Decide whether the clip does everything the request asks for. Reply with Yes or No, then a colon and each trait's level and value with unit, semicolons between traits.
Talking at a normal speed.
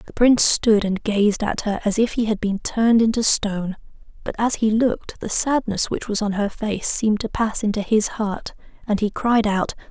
No: fast, 220 wpm